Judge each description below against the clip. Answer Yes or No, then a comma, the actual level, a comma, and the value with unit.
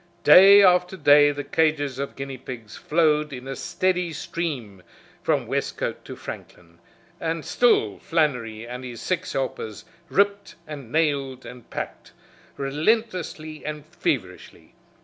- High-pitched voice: No, medium, 150 Hz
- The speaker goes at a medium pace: No, slow, 125 wpm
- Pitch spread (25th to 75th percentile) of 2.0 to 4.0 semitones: No, average, 4.5 semitones